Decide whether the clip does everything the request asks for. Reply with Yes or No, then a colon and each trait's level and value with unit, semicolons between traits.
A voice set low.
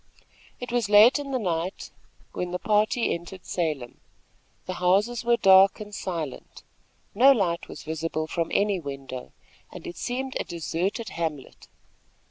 No: medium, 185 Hz